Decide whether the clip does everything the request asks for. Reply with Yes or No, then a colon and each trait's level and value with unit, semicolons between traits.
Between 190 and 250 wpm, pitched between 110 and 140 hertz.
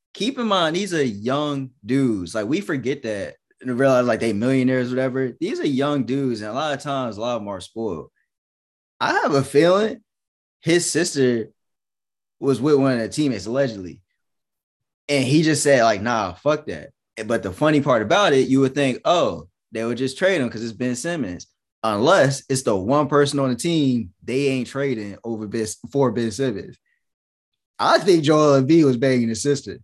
Yes: average, 195 wpm; low, 135 Hz